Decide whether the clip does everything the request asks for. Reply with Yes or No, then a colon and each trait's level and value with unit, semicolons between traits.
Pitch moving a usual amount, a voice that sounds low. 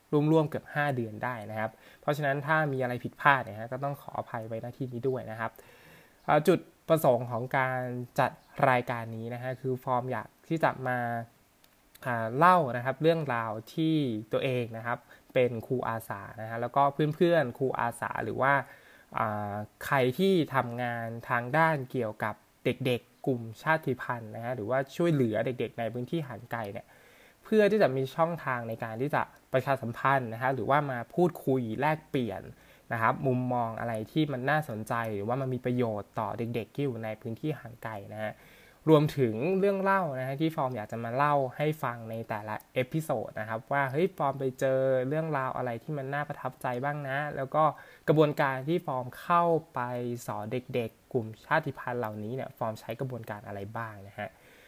Yes: average, 4.0 semitones; low, 125 Hz